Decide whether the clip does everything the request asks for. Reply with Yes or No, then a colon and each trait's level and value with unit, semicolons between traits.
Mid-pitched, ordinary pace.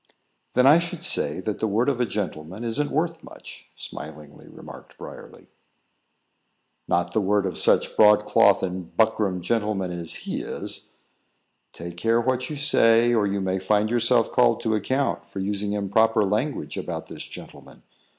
No: low, 105 Hz; average, 160 wpm